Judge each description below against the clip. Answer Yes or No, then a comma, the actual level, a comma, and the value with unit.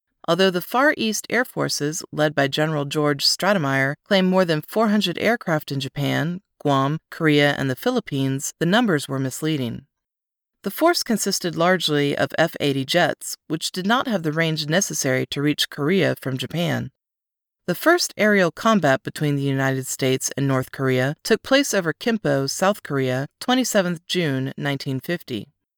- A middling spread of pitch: No, wide, 5.9 semitones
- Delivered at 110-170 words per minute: Yes, average, 155 wpm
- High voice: No, medium, 155 Hz